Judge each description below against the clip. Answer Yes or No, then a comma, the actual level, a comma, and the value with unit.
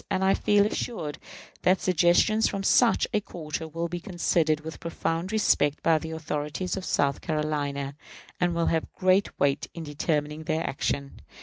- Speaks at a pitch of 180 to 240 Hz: No, medium, 165 Hz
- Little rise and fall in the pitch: No, average, 3.5 semitones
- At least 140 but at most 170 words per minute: Yes, average, 165 wpm